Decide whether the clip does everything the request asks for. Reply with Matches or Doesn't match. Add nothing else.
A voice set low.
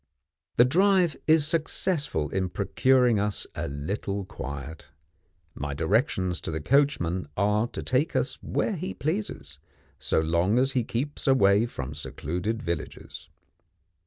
Matches